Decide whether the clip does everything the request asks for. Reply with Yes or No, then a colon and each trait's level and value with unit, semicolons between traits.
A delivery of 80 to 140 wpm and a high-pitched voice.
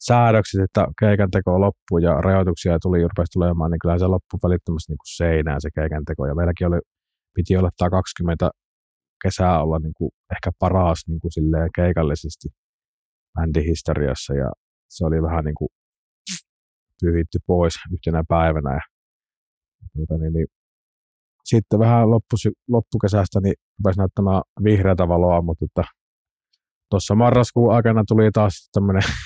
No: average, 125 wpm; very low, 90 Hz